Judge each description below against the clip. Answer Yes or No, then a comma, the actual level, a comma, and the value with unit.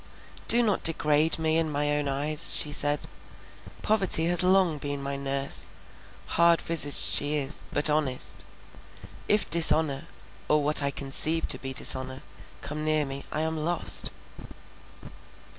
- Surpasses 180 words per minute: No, average, 140 wpm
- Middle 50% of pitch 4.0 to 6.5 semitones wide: No, narrow, 2.4 semitones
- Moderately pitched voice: Yes, medium, 150 Hz